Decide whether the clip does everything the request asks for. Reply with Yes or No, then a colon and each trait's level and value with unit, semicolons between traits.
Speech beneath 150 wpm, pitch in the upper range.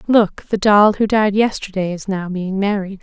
No: average, 200 wpm; high, 200 Hz